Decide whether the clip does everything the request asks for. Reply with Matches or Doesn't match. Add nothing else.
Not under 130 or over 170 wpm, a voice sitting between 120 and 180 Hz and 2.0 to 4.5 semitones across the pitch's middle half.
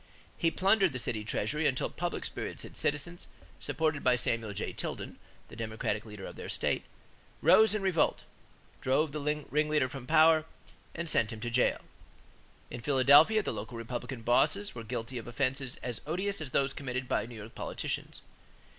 Doesn't match